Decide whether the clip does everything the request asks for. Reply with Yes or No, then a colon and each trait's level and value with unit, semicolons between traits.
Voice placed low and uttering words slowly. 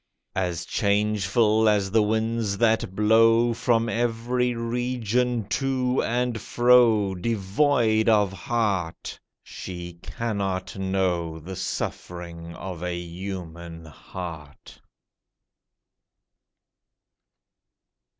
Yes: low, 105 Hz; slow, 80 wpm